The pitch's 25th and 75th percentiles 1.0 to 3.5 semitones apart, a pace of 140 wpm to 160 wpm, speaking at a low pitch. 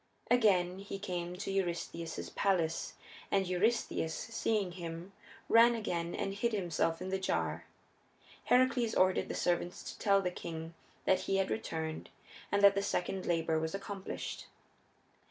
No: average, 2.8 semitones; average, 145 wpm; high, 190 Hz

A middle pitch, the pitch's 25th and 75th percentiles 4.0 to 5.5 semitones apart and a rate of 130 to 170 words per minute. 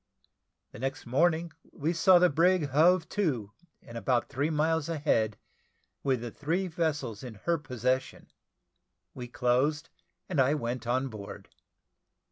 Yes: medium, 145 Hz; average, 4.8 semitones; average, 140 wpm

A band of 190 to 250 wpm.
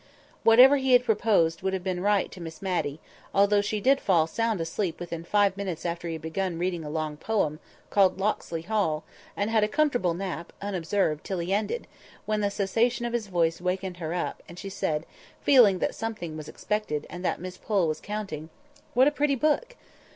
Yes: average, 195 wpm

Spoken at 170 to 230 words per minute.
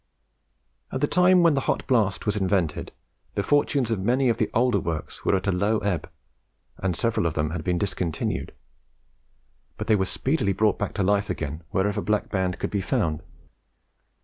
Yes: average, 180 wpm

